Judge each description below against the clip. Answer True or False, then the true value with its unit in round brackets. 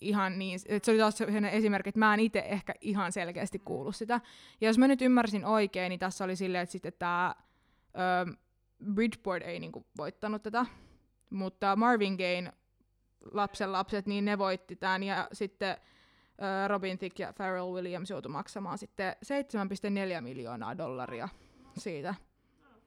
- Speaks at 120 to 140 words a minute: False (150 wpm)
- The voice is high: True (195 Hz)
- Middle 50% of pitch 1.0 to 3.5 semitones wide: True (2.4 semitones)